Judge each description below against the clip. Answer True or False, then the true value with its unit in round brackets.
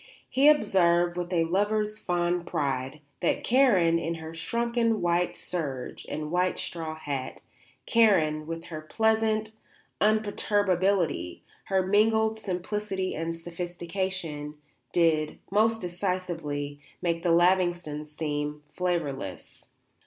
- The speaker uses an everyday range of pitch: True (4.4 semitones)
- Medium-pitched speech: True (175 Hz)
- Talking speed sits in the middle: False (110 wpm)